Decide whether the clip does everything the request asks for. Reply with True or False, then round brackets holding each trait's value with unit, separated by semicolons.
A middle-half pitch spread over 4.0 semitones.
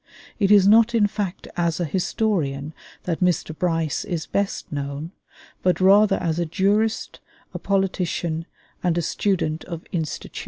False (3.6 semitones)